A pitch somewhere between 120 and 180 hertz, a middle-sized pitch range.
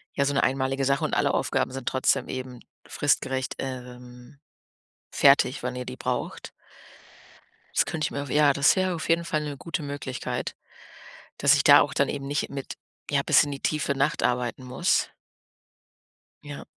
No: medium, 140 Hz; narrow, 2.0 semitones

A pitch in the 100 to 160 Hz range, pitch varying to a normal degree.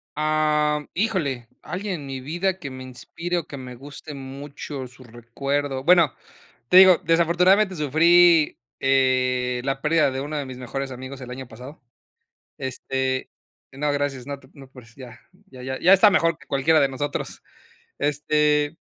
Yes: medium, 140 Hz; average, 3.3 semitones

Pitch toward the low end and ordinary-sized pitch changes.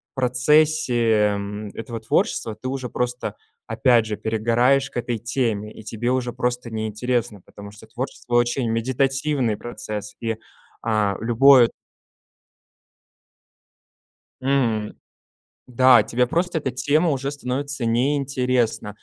Yes: low, 120 Hz; average, 3.0 semitones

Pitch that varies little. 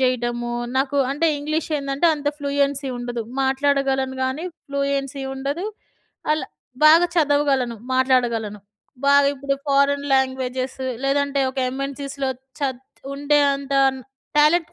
Yes: narrow, 1.5 semitones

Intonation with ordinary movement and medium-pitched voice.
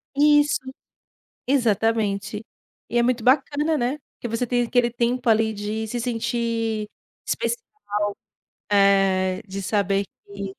No: average, 3.3 semitones; high, 225 Hz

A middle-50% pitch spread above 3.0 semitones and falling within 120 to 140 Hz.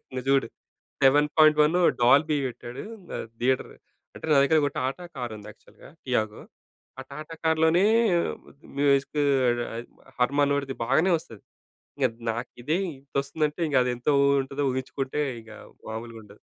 Yes: average, 3.4 semitones; low, 135 Hz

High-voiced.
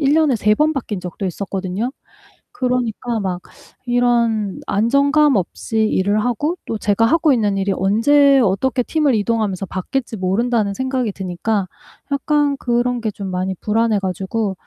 Yes: high, 225 Hz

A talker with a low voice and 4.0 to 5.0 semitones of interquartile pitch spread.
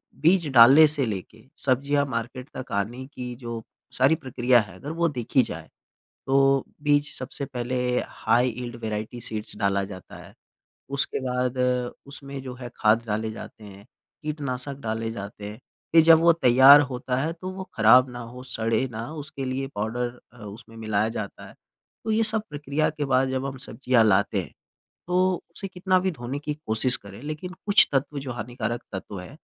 Yes: low, 130 Hz; average, 4.3 semitones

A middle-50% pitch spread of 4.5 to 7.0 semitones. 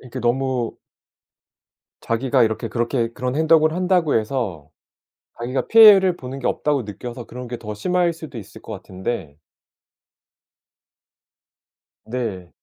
Yes: wide, 5.4 semitones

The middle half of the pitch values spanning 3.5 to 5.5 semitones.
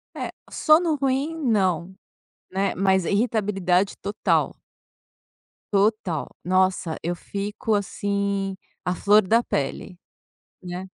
No: narrow, 2.4 semitones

